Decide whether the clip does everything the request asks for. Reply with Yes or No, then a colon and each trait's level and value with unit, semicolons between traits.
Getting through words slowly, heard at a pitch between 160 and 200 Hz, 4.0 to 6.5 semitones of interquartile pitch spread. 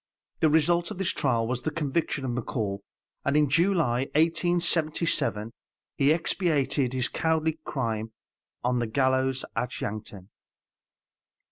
No: slow, 125 wpm; medium, 140 Hz; average, 5.0 semitones